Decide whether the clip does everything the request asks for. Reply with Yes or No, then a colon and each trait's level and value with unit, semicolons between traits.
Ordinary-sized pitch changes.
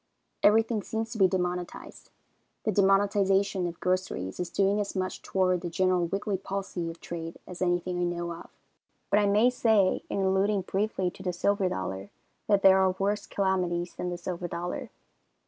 No: narrow, 2.1 semitones